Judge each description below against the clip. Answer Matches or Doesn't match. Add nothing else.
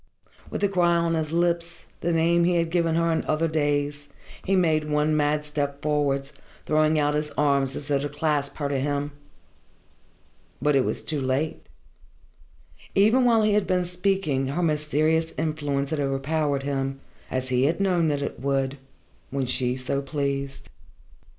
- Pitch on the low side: Doesn't match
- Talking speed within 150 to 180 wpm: Matches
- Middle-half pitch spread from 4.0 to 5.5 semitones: Doesn't match